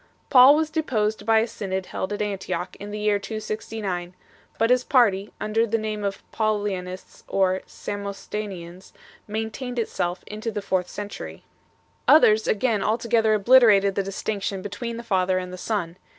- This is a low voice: No, high, 210 Hz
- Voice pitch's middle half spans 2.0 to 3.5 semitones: Yes, narrow, 2.6 semitones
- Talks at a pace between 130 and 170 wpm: Yes, average, 155 wpm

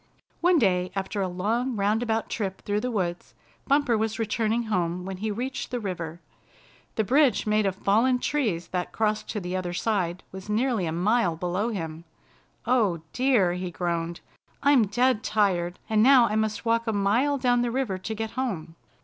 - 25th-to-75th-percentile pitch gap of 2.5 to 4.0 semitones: No, average, 4.6 semitones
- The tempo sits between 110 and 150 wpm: No, average, 180 wpm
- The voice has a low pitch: No, high, 210 Hz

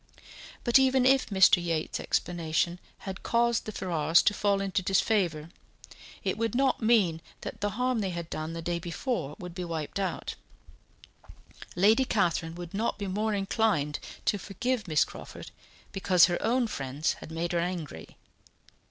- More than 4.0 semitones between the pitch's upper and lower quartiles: Yes, average, 4.7 semitones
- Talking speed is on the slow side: No, average, 160 wpm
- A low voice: No, medium, 185 Hz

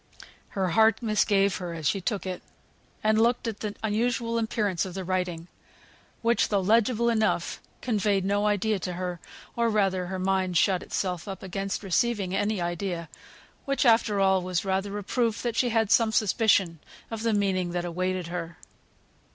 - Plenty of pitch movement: No, average, 3.2 semitones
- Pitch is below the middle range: No, high, 195 Hz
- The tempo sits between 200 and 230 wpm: No, average, 165 wpm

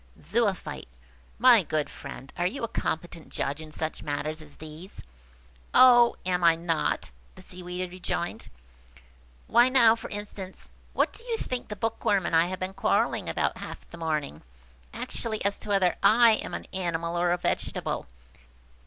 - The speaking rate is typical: Yes, average, 160 wpm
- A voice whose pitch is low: No, medium, 180 Hz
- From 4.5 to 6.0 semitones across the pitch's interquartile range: Yes, average, 4.8 semitones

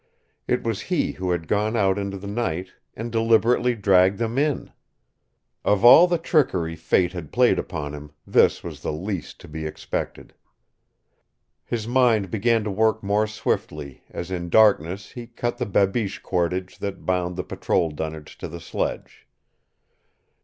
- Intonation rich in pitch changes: No, average, 4.6 semitones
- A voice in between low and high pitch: No, low, 100 Hz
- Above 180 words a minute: No, average, 160 wpm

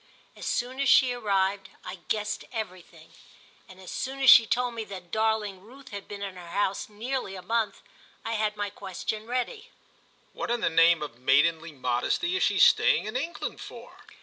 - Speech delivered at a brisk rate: No, average, 185 wpm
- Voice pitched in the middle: No, high, 210 Hz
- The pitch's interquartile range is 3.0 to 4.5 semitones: No, average, 4.9 semitones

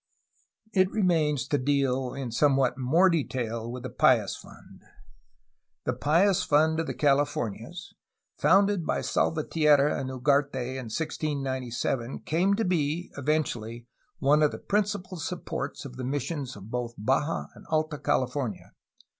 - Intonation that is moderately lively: Yes, average, 4.0 semitones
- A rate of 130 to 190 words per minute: Yes, average, 145 wpm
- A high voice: No, medium, 145 Hz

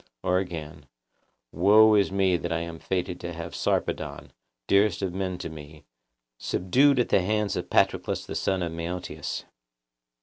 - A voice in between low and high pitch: No, very low, 90 Hz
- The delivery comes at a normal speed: Yes, average, 160 wpm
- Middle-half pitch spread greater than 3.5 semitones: No, average, 2.9 semitones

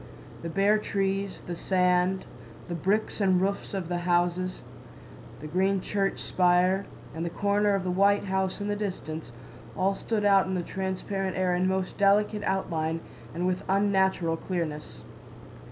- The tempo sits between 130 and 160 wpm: Yes, average, 155 wpm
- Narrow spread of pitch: Yes, narrow, 1.9 semitones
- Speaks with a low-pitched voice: No, high, 190 Hz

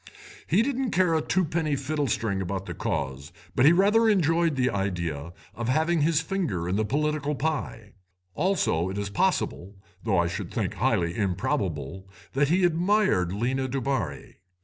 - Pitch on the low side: Yes, low, 130 Hz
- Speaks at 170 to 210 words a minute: No, average, 155 wpm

